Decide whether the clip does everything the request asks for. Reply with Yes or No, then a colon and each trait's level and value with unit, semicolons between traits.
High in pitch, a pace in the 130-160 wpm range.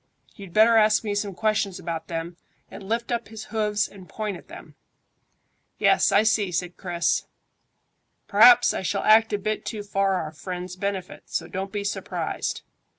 No: high, 200 Hz; average, 170 wpm